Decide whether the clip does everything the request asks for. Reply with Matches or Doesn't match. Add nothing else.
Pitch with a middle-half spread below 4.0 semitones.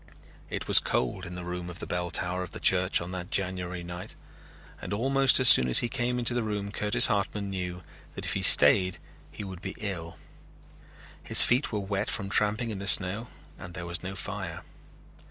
Matches